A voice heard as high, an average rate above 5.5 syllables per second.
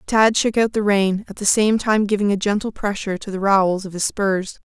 No: high, 205 Hz; 5.4 syllables/s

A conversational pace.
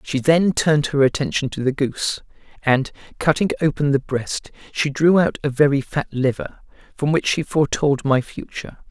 Yes: average, 175 wpm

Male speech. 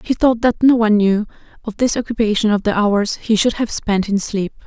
No: female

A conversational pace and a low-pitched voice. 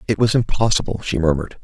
Yes: average, 185 wpm; low, 100 Hz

